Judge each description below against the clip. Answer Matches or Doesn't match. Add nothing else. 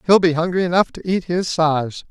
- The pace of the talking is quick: Matches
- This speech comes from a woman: Doesn't match